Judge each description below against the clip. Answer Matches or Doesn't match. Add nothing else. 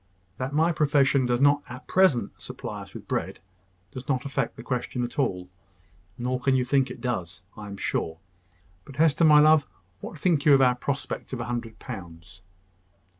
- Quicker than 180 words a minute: Matches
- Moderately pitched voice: Doesn't match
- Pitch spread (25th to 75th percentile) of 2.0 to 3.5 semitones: Matches